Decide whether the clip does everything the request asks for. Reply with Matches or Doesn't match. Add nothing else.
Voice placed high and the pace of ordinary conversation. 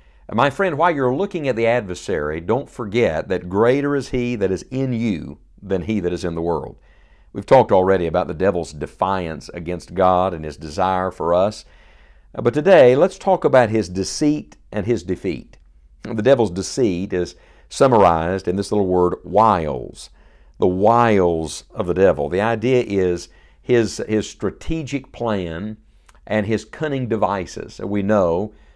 Doesn't match